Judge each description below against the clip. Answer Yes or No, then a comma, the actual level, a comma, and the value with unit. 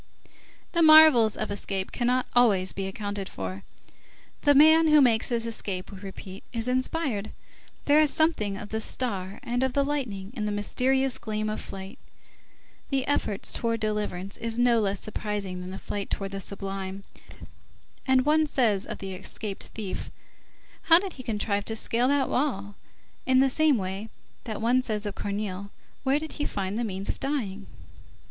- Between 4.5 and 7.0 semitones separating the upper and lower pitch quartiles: Yes, average, 4.9 semitones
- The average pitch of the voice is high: Yes, high, 220 Hz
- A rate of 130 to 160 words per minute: No, average, 170 wpm